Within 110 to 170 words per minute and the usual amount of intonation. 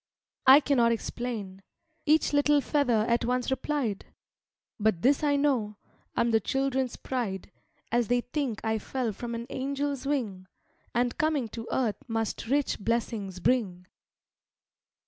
Yes: slow, 135 wpm; average, 3.8 semitones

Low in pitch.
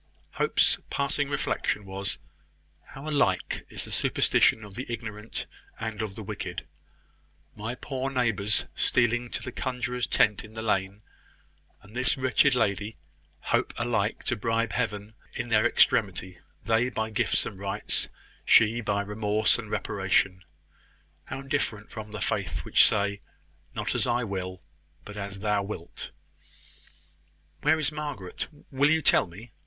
Yes: low, 110 Hz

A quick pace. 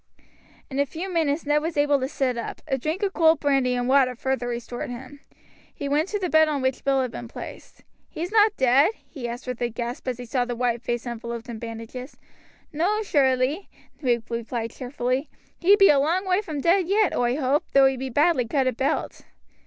Yes: fast, 210 wpm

